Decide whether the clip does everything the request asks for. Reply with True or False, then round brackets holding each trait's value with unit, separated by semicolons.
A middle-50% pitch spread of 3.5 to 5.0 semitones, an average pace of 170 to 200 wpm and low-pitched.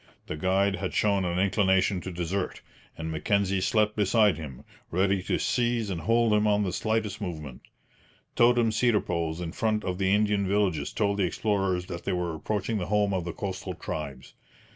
False (2.9 semitones; 185 wpm; 95 Hz)